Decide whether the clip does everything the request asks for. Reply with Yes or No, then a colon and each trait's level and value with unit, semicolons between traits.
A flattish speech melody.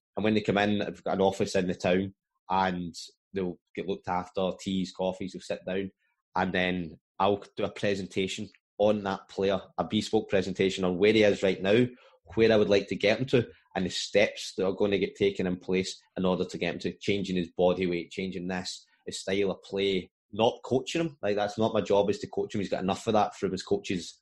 Yes: narrow, 2.0 semitones